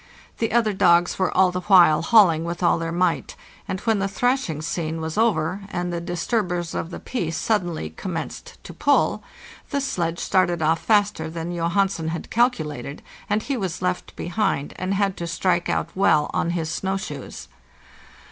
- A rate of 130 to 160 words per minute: No, average, 175 wpm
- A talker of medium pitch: Yes, medium, 175 Hz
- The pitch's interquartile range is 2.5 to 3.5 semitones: Yes, average, 3.2 semitones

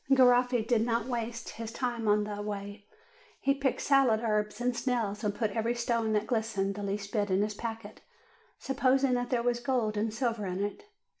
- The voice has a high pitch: Yes, high, 225 Hz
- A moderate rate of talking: Yes, average, 195 wpm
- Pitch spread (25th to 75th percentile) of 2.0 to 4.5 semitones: Yes, average, 2.8 semitones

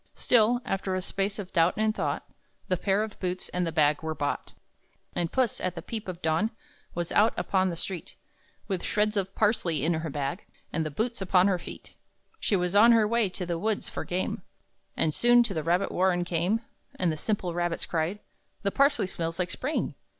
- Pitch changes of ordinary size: Yes, average, 3.8 semitones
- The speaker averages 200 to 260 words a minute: Yes, fast, 205 wpm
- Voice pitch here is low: No, medium, 185 Hz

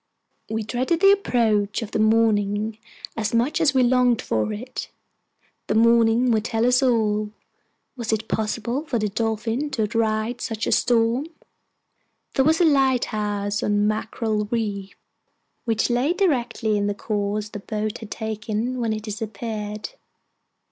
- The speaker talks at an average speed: Yes, average, 150 wpm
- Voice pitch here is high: Yes, high, 225 Hz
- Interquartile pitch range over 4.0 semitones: No, narrow, 2.5 semitones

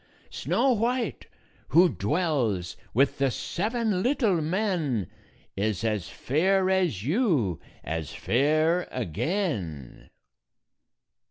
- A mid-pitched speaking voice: Yes, medium, 155 Hz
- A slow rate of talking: Yes, slow, 90 wpm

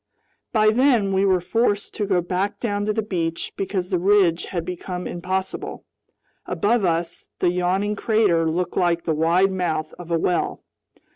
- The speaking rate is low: No, average, 165 wpm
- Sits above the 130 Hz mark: Yes, medium, 185 Hz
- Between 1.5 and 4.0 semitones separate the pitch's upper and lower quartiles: Yes, average, 2.9 semitones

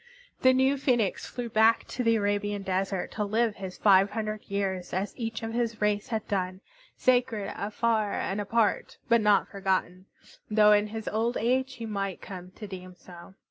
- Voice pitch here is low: No, high, 210 Hz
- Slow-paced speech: No, average, 180 wpm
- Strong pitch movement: No, average, 2.7 semitones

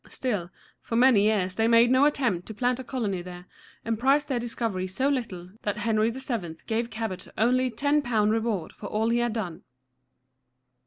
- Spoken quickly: No, average, 175 wpm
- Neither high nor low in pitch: No, high, 225 Hz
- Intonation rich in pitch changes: No, average, 3.4 semitones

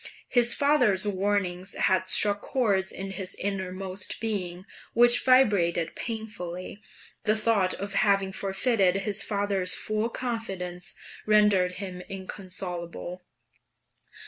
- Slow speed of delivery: Yes, slow, 105 wpm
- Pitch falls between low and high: No, high, 195 Hz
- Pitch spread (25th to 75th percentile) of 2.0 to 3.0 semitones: Yes, narrow, 2.6 semitones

